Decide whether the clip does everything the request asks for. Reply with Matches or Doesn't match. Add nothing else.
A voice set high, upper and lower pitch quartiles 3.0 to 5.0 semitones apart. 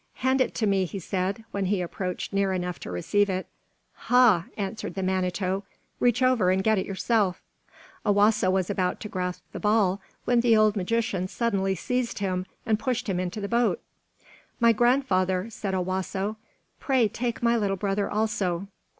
Matches